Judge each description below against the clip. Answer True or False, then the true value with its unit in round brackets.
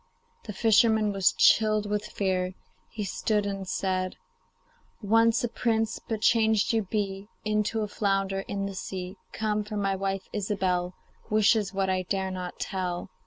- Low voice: False (200 Hz)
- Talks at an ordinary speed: True (155 wpm)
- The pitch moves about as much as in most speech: False (2.1 semitones)